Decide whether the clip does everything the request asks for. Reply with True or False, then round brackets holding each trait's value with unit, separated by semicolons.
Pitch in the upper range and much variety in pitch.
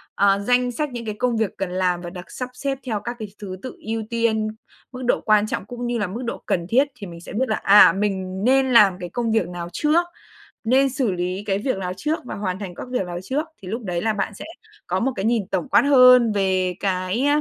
False (215 Hz; 4.8 semitones)